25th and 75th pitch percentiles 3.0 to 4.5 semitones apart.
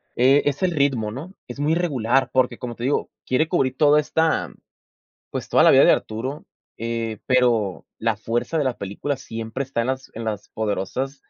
Yes: average, 3.8 semitones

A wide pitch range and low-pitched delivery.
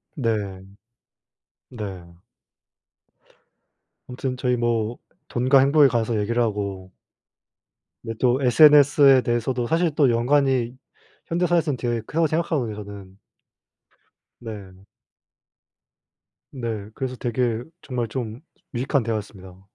No: average, 3.9 semitones; low, 120 Hz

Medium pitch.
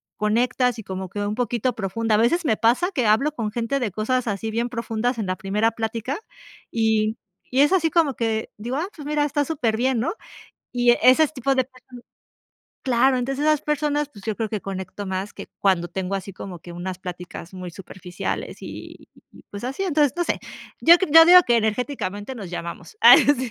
No: high, 230 Hz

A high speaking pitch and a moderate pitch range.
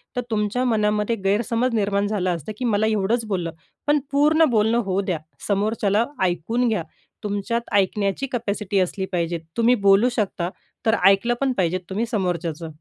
Yes: high, 210 Hz; average, 3.2 semitones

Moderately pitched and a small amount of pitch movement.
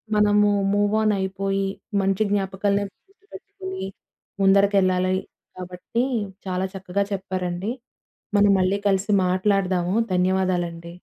No: high, 195 Hz; narrow, 1.8 semitones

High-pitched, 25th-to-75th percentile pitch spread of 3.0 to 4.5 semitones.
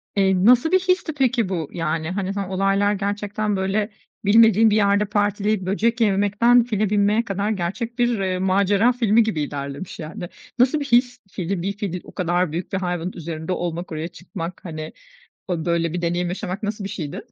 Yes: high, 195 Hz; average, 3.5 semitones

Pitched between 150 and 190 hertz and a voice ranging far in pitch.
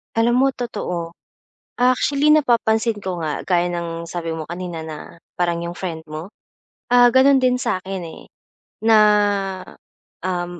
Yes: medium, 185 Hz; wide, 6.0 semitones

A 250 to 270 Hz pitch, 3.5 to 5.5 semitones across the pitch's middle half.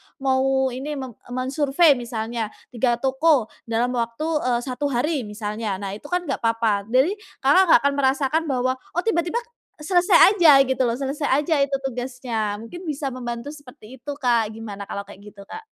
Yes: very high, 260 Hz; average, 3.9 semitones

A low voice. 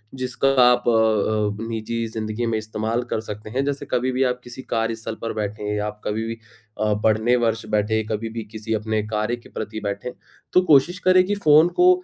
Yes: low, 110 Hz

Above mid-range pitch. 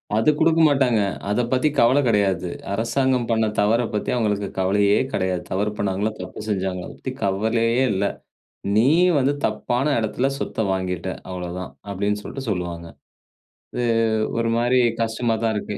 No: low, 105 Hz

